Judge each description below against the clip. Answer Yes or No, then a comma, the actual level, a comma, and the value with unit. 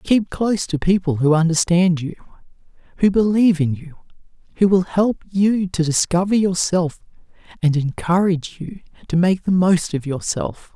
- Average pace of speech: Yes, average, 150 wpm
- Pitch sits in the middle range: Yes, medium, 175 Hz